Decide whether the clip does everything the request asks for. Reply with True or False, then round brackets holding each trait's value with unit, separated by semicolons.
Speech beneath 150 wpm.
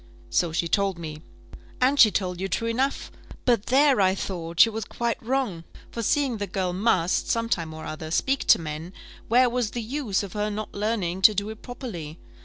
False (205 wpm)